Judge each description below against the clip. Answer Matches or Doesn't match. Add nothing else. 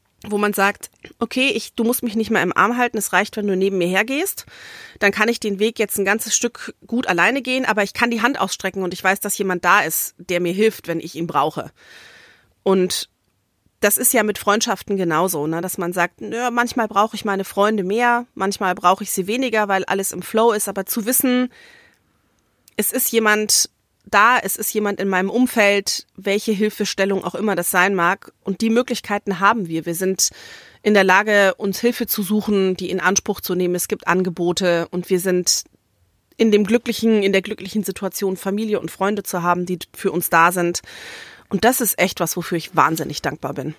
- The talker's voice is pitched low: Doesn't match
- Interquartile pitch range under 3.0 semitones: Doesn't match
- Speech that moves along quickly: Matches